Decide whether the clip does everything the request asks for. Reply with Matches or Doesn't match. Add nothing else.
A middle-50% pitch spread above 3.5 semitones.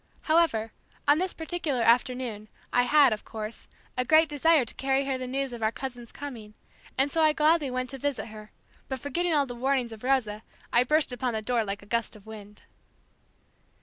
Matches